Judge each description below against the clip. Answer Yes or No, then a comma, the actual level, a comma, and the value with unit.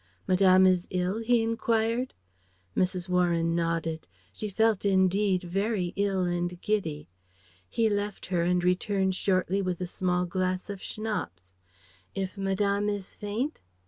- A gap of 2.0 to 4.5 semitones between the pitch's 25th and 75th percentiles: Yes, narrow, 2.4 semitones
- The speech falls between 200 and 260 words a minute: No, slow, 135 wpm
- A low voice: No, high, 190 Hz